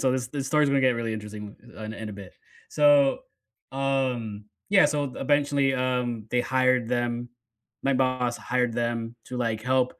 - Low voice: Yes, low, 125 Hz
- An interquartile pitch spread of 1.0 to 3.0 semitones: Yes, narrow, 2.6 semitones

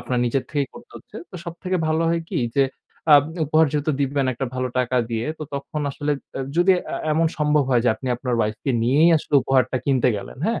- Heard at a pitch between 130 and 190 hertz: Yes, medium, 140 Hz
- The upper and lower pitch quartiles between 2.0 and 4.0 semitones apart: Yes, average, 3.6 semitones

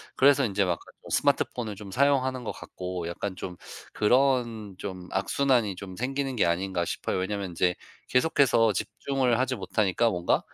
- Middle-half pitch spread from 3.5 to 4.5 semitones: No, wide, 5.6 semitones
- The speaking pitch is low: Yes, low, 105 Hz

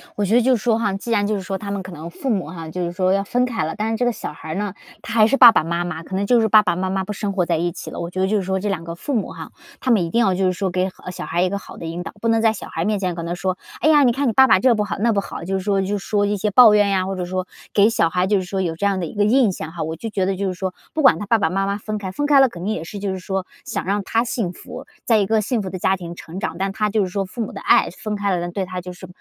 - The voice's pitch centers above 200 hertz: No, high, 195 Hz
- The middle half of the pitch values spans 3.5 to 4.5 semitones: No, average, 2.8 semitones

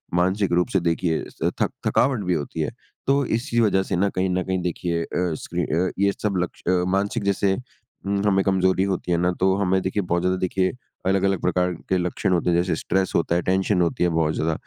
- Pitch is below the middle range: Yes, very low, 95 Hz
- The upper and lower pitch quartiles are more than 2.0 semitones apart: No, narrow, 1.7 semitones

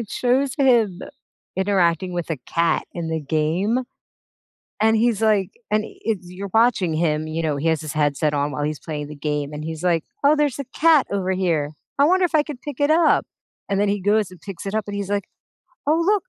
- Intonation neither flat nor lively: No, wide, 6.4 semitones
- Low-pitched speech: No, high, 190 Hz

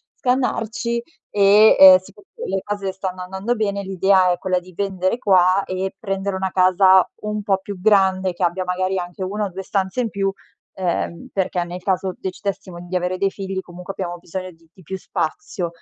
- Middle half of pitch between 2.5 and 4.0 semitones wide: No, narrow, 1.5 semitones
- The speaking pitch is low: No, high, 190 Hz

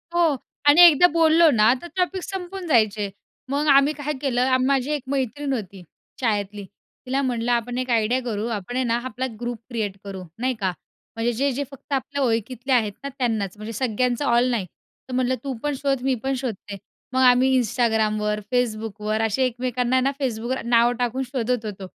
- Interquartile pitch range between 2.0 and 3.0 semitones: No, average, 3.5 semitones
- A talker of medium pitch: No, high, 245 Hz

